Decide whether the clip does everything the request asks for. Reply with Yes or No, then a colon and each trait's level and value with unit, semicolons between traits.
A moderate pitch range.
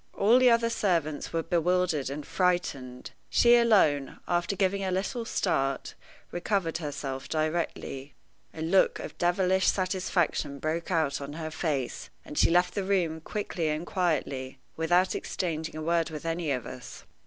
Yes: average, 3.7 semitones